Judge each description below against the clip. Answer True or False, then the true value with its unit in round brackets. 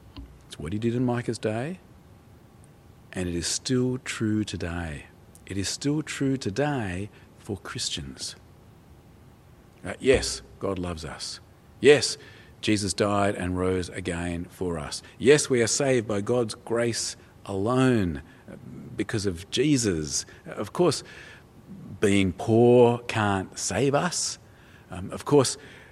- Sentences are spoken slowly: True (125 wpm)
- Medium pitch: False (105 Hz)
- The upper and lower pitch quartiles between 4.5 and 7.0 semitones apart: True (4.8 semitones)